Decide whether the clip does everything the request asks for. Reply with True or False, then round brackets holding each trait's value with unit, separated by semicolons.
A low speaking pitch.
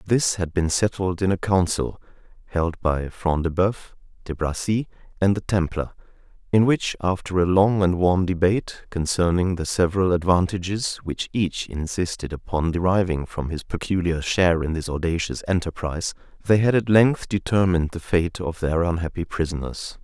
True (90 Hz)